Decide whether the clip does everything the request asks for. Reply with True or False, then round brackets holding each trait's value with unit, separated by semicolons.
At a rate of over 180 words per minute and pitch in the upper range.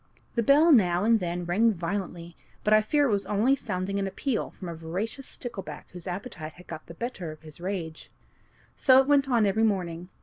True (205 wpm; 195 Hz)